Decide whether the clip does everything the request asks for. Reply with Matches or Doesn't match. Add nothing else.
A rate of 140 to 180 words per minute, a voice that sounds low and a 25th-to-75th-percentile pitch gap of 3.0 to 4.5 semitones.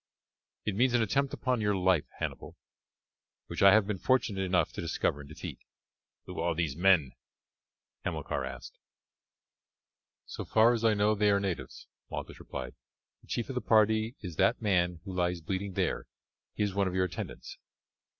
Matches